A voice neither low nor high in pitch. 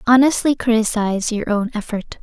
No: high, 225 Hz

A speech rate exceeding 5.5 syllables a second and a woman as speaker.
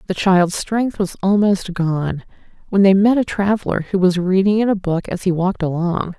No: 5.1 syllables/s; female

